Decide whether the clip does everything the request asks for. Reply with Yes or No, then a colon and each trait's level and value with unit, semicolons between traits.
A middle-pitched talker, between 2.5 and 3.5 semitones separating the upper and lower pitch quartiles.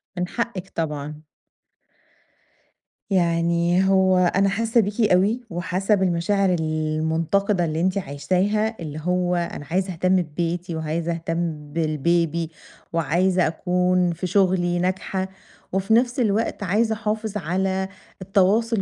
Yes: medium, 180 Hz; average, 2.8 semitones